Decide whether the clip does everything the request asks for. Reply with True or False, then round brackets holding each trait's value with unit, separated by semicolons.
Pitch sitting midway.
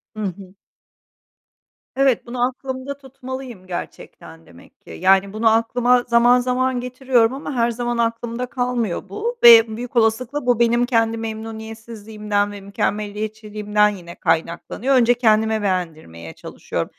False (230 Hz)